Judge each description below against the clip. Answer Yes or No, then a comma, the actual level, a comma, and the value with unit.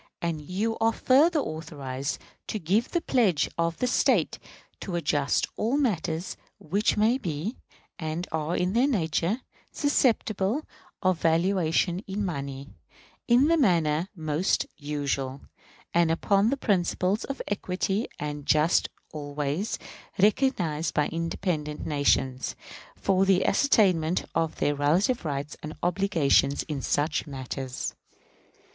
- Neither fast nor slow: No, slow, 125 wpm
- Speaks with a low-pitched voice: No, medium, 170 Hz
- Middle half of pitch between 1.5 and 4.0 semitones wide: No, wide, 5.4 semitones